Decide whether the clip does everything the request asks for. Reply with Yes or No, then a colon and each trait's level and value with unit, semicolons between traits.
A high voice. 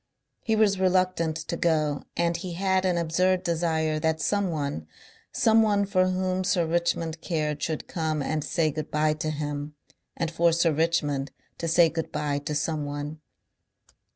No: medium, 165 Hz